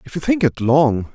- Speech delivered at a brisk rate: Yes, fast, 265 wpm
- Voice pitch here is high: No, low, 135 Hz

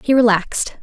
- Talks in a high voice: Yes, high, 225 Hz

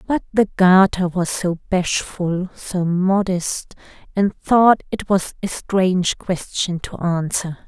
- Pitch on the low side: No, medium, 185 Hz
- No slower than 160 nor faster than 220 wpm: No, slow, 135 wpm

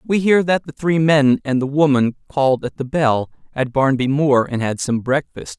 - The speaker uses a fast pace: Yes, fast, 215 wpm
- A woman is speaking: No, male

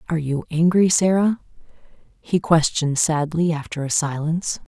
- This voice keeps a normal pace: No, slow, 125 wpm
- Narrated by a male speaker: No, female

